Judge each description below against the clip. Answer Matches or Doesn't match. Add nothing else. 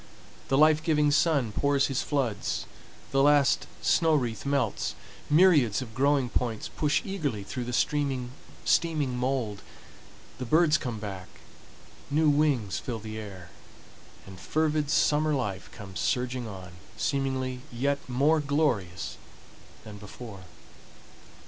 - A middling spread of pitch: Matches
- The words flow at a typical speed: Doesn't match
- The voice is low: Matches